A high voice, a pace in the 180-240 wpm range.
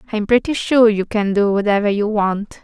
Yes: high, 210 Hz; fast, 205 wpm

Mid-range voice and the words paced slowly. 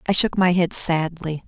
No: medium, 170 Hz; fast, 205 wpm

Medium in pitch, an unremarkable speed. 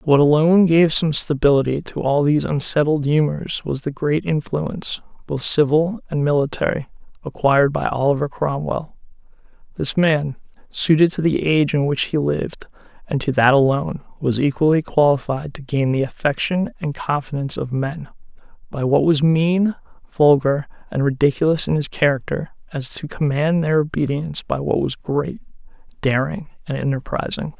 Yes: medium, 145 Hz; average, 150 wpm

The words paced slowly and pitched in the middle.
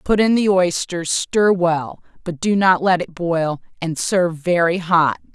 No: average, 180 wpm; medium, 175 Hz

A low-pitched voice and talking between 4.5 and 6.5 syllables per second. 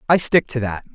Yes: low, 130 Hz; 5.8 syllables/s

